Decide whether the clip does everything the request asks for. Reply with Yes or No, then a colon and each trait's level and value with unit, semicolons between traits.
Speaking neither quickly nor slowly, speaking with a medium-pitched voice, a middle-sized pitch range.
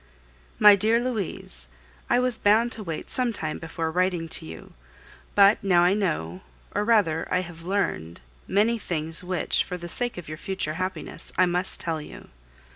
Yes: average, 175 wpm; medium, 180 Hz; average, 4.3 semitones